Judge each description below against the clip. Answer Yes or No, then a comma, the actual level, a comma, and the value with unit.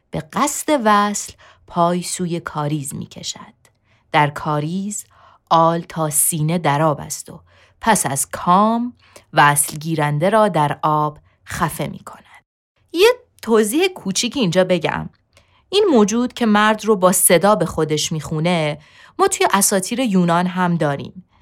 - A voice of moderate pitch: Yes, medium, 175 Hz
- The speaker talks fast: No, average, 135 wpm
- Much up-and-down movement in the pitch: Yes, wide, 6.0 semitones